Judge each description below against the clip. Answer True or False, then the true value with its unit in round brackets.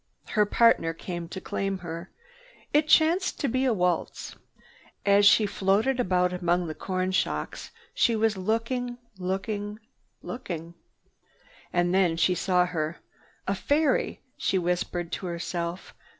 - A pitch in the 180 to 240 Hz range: True (185 Hz)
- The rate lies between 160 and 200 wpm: False (135 wpm)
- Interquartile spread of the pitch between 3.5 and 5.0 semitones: True (3.9 semitones)